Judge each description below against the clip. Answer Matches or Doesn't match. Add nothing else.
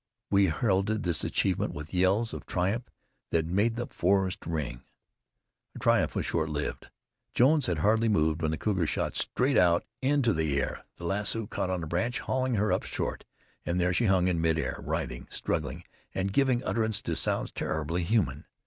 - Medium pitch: Doesn't match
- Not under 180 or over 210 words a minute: Matches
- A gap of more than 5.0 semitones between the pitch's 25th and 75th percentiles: Matches